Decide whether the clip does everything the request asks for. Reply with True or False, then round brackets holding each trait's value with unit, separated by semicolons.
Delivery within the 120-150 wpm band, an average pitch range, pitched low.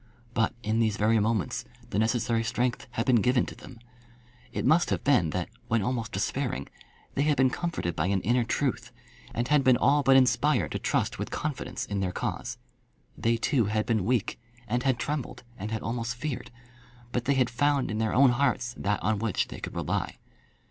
False (195 wpm; 3.2 semitones; 120 Hz)